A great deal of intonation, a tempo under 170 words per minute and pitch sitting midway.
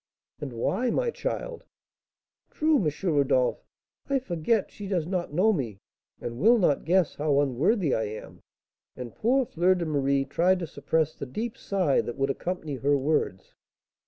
Yes: wide, 6.3 semitones; average, 160 wpm; medium, 160 Hz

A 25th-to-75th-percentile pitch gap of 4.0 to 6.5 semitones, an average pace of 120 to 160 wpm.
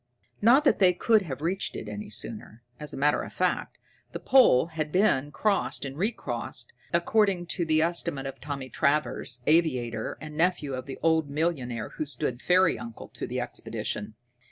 No: average, 5.0 semitones; average, 180 wpm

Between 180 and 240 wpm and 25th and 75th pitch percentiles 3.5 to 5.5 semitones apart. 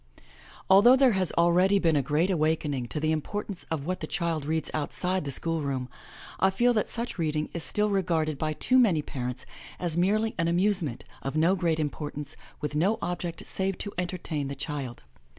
Yes: average, 185 wpm; average, 4.2 semitones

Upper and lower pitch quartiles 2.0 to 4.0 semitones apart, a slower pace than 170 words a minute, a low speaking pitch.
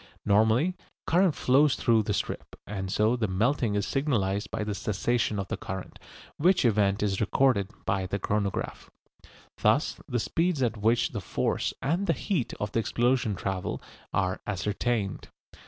No: average, 4.4 semitones; average, 155 wpm; low, 110 Hz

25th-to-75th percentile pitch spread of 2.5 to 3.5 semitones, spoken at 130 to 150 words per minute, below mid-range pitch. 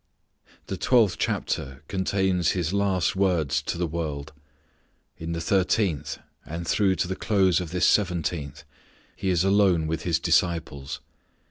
Yes: average, 3.0 semitones; average, 140 wpm; very low, 90 Hz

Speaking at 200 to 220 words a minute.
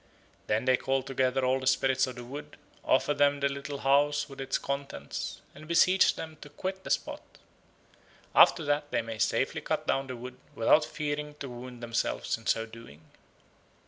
No: average, 180 wpm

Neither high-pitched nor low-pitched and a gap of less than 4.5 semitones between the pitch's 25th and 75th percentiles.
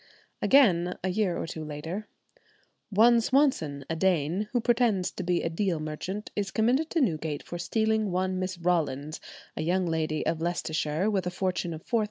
No: medium, 180 Hz; average, 4.8 semitones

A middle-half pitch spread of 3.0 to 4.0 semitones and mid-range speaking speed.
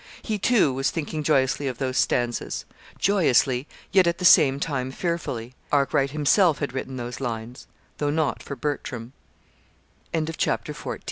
Yes: average, 3.7 semitones; average, 150 wpm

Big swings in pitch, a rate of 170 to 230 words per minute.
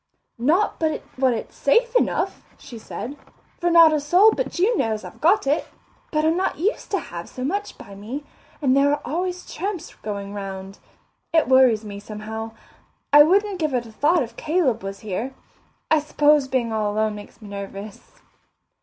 Yes: wide, 7.5 semitones; average, 180 wpm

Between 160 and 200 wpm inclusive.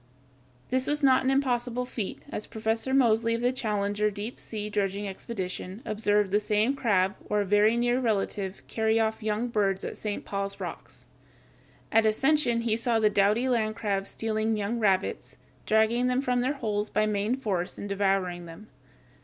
Yes: average, 170 wpm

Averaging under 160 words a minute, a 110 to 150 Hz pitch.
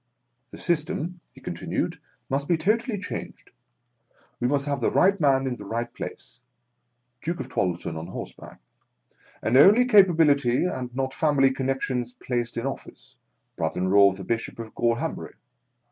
No: average, 170 wpm; low, 135 Hz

